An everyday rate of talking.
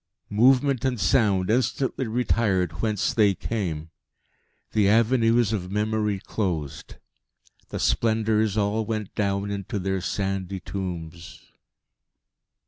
No: slow, 105 wpm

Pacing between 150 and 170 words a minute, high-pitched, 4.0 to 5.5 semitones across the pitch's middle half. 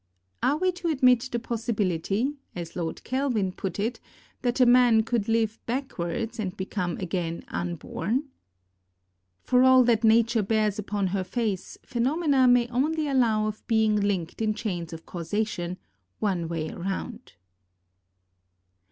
No: slow, 135 wpm; high, 220 Hz; average, 4.7 semitones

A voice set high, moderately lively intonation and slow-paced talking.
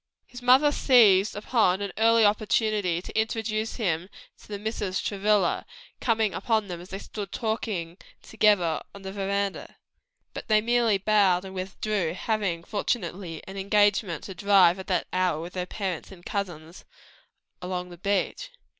No: high, 200 Hz; average, 3.0 semitones; average, 150 wpm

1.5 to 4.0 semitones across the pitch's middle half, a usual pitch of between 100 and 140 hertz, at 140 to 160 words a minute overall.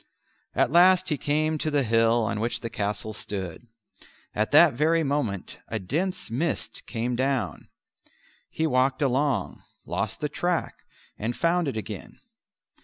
No: wide, 5.6 semitones; low, 135 Hz; average, 145 wpm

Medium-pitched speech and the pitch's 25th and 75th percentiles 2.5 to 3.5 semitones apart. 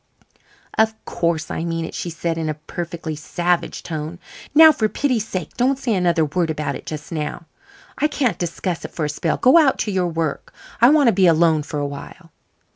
No: medium, 170 Hz; average, 5.3 semitones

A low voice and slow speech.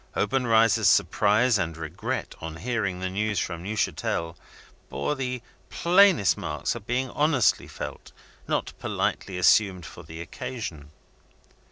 Yes: low, 105 Hz; slow, 125 wpm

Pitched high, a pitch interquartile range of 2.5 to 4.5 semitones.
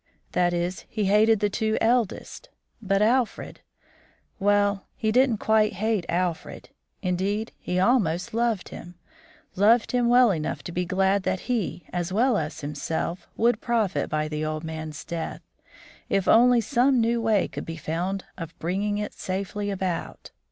Yes: high, 200 Hz; average, 4.2 semitones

